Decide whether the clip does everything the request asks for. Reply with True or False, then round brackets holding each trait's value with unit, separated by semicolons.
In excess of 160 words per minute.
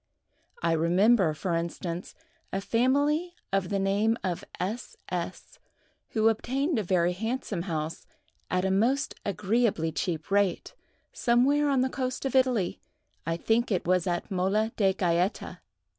False (140 wpm)